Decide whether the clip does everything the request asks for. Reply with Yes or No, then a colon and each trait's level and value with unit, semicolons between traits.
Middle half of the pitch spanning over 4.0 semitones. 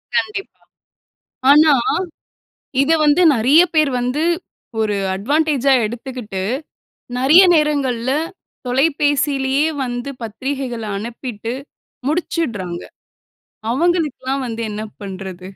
Yes: average, 4.6 semitones